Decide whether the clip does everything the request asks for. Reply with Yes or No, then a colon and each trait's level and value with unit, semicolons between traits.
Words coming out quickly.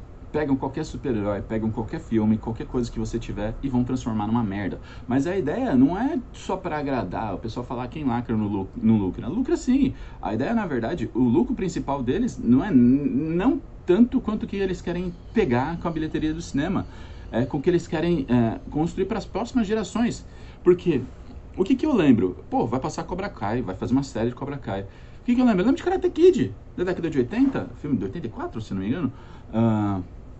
Yes: fast, 215 wpm